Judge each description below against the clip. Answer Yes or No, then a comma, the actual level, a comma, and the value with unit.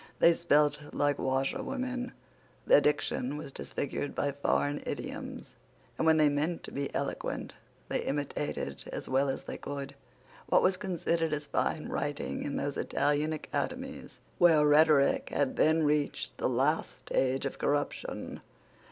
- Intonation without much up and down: Yes, narrow, 2.2 semitones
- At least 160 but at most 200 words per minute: No, average, 145 wpm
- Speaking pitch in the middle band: Yes, medium, 145 Hz